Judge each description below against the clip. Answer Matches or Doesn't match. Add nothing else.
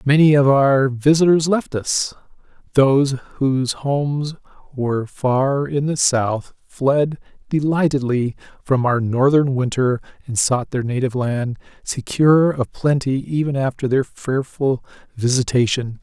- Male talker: Matches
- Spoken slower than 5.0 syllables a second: Matches